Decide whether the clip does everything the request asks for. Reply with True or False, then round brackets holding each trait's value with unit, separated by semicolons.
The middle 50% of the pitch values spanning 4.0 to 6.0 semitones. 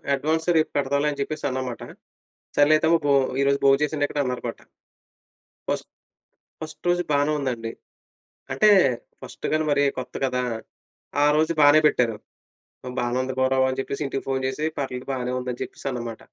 False (2.8 semitones)